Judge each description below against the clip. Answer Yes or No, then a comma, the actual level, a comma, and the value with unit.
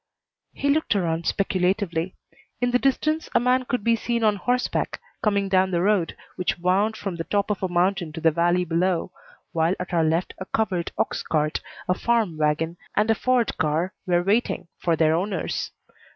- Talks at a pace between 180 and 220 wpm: Yes, average, 185 wpm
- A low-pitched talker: No, medium, 185 Hz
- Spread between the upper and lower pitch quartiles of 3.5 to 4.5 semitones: Yes, average, 4.1 semitones